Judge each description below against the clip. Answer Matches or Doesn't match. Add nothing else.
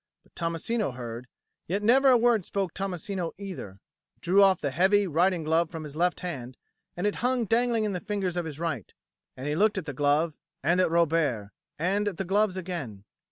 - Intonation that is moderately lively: Matches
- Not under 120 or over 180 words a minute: Doesn't match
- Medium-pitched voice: Matches